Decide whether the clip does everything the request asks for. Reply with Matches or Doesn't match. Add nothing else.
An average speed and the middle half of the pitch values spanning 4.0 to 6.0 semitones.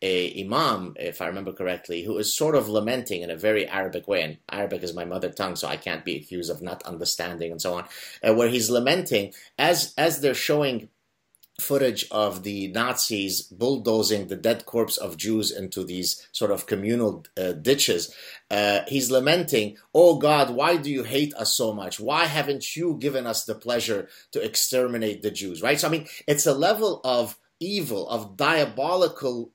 Matches